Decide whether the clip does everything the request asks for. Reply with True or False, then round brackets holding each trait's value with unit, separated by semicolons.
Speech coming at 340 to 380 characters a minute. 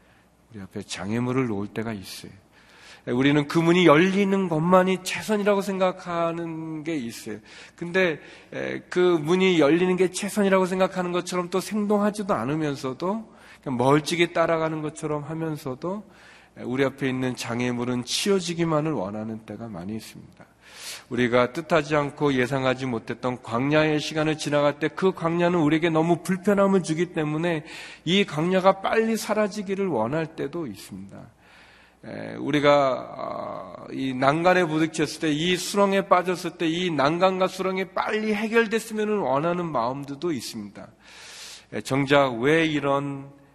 False (315 characters per minute)